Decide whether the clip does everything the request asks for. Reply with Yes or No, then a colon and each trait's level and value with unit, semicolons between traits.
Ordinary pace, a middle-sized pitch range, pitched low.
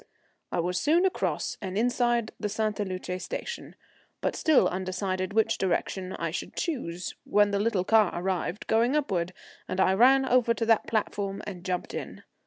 No: average, 170 wpm; average, 4.0 semitones; high, 205 Hz